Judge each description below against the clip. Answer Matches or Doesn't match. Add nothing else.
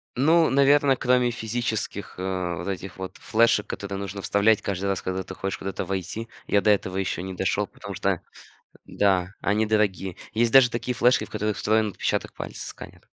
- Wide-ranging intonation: Doesn't match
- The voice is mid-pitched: Doesn't match